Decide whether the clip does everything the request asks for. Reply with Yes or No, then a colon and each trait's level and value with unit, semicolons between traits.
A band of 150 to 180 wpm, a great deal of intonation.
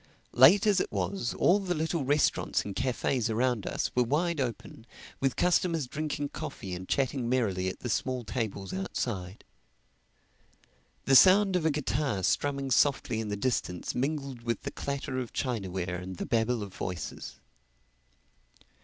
Yes: average, 155 wpm; wide, 5.9 semitones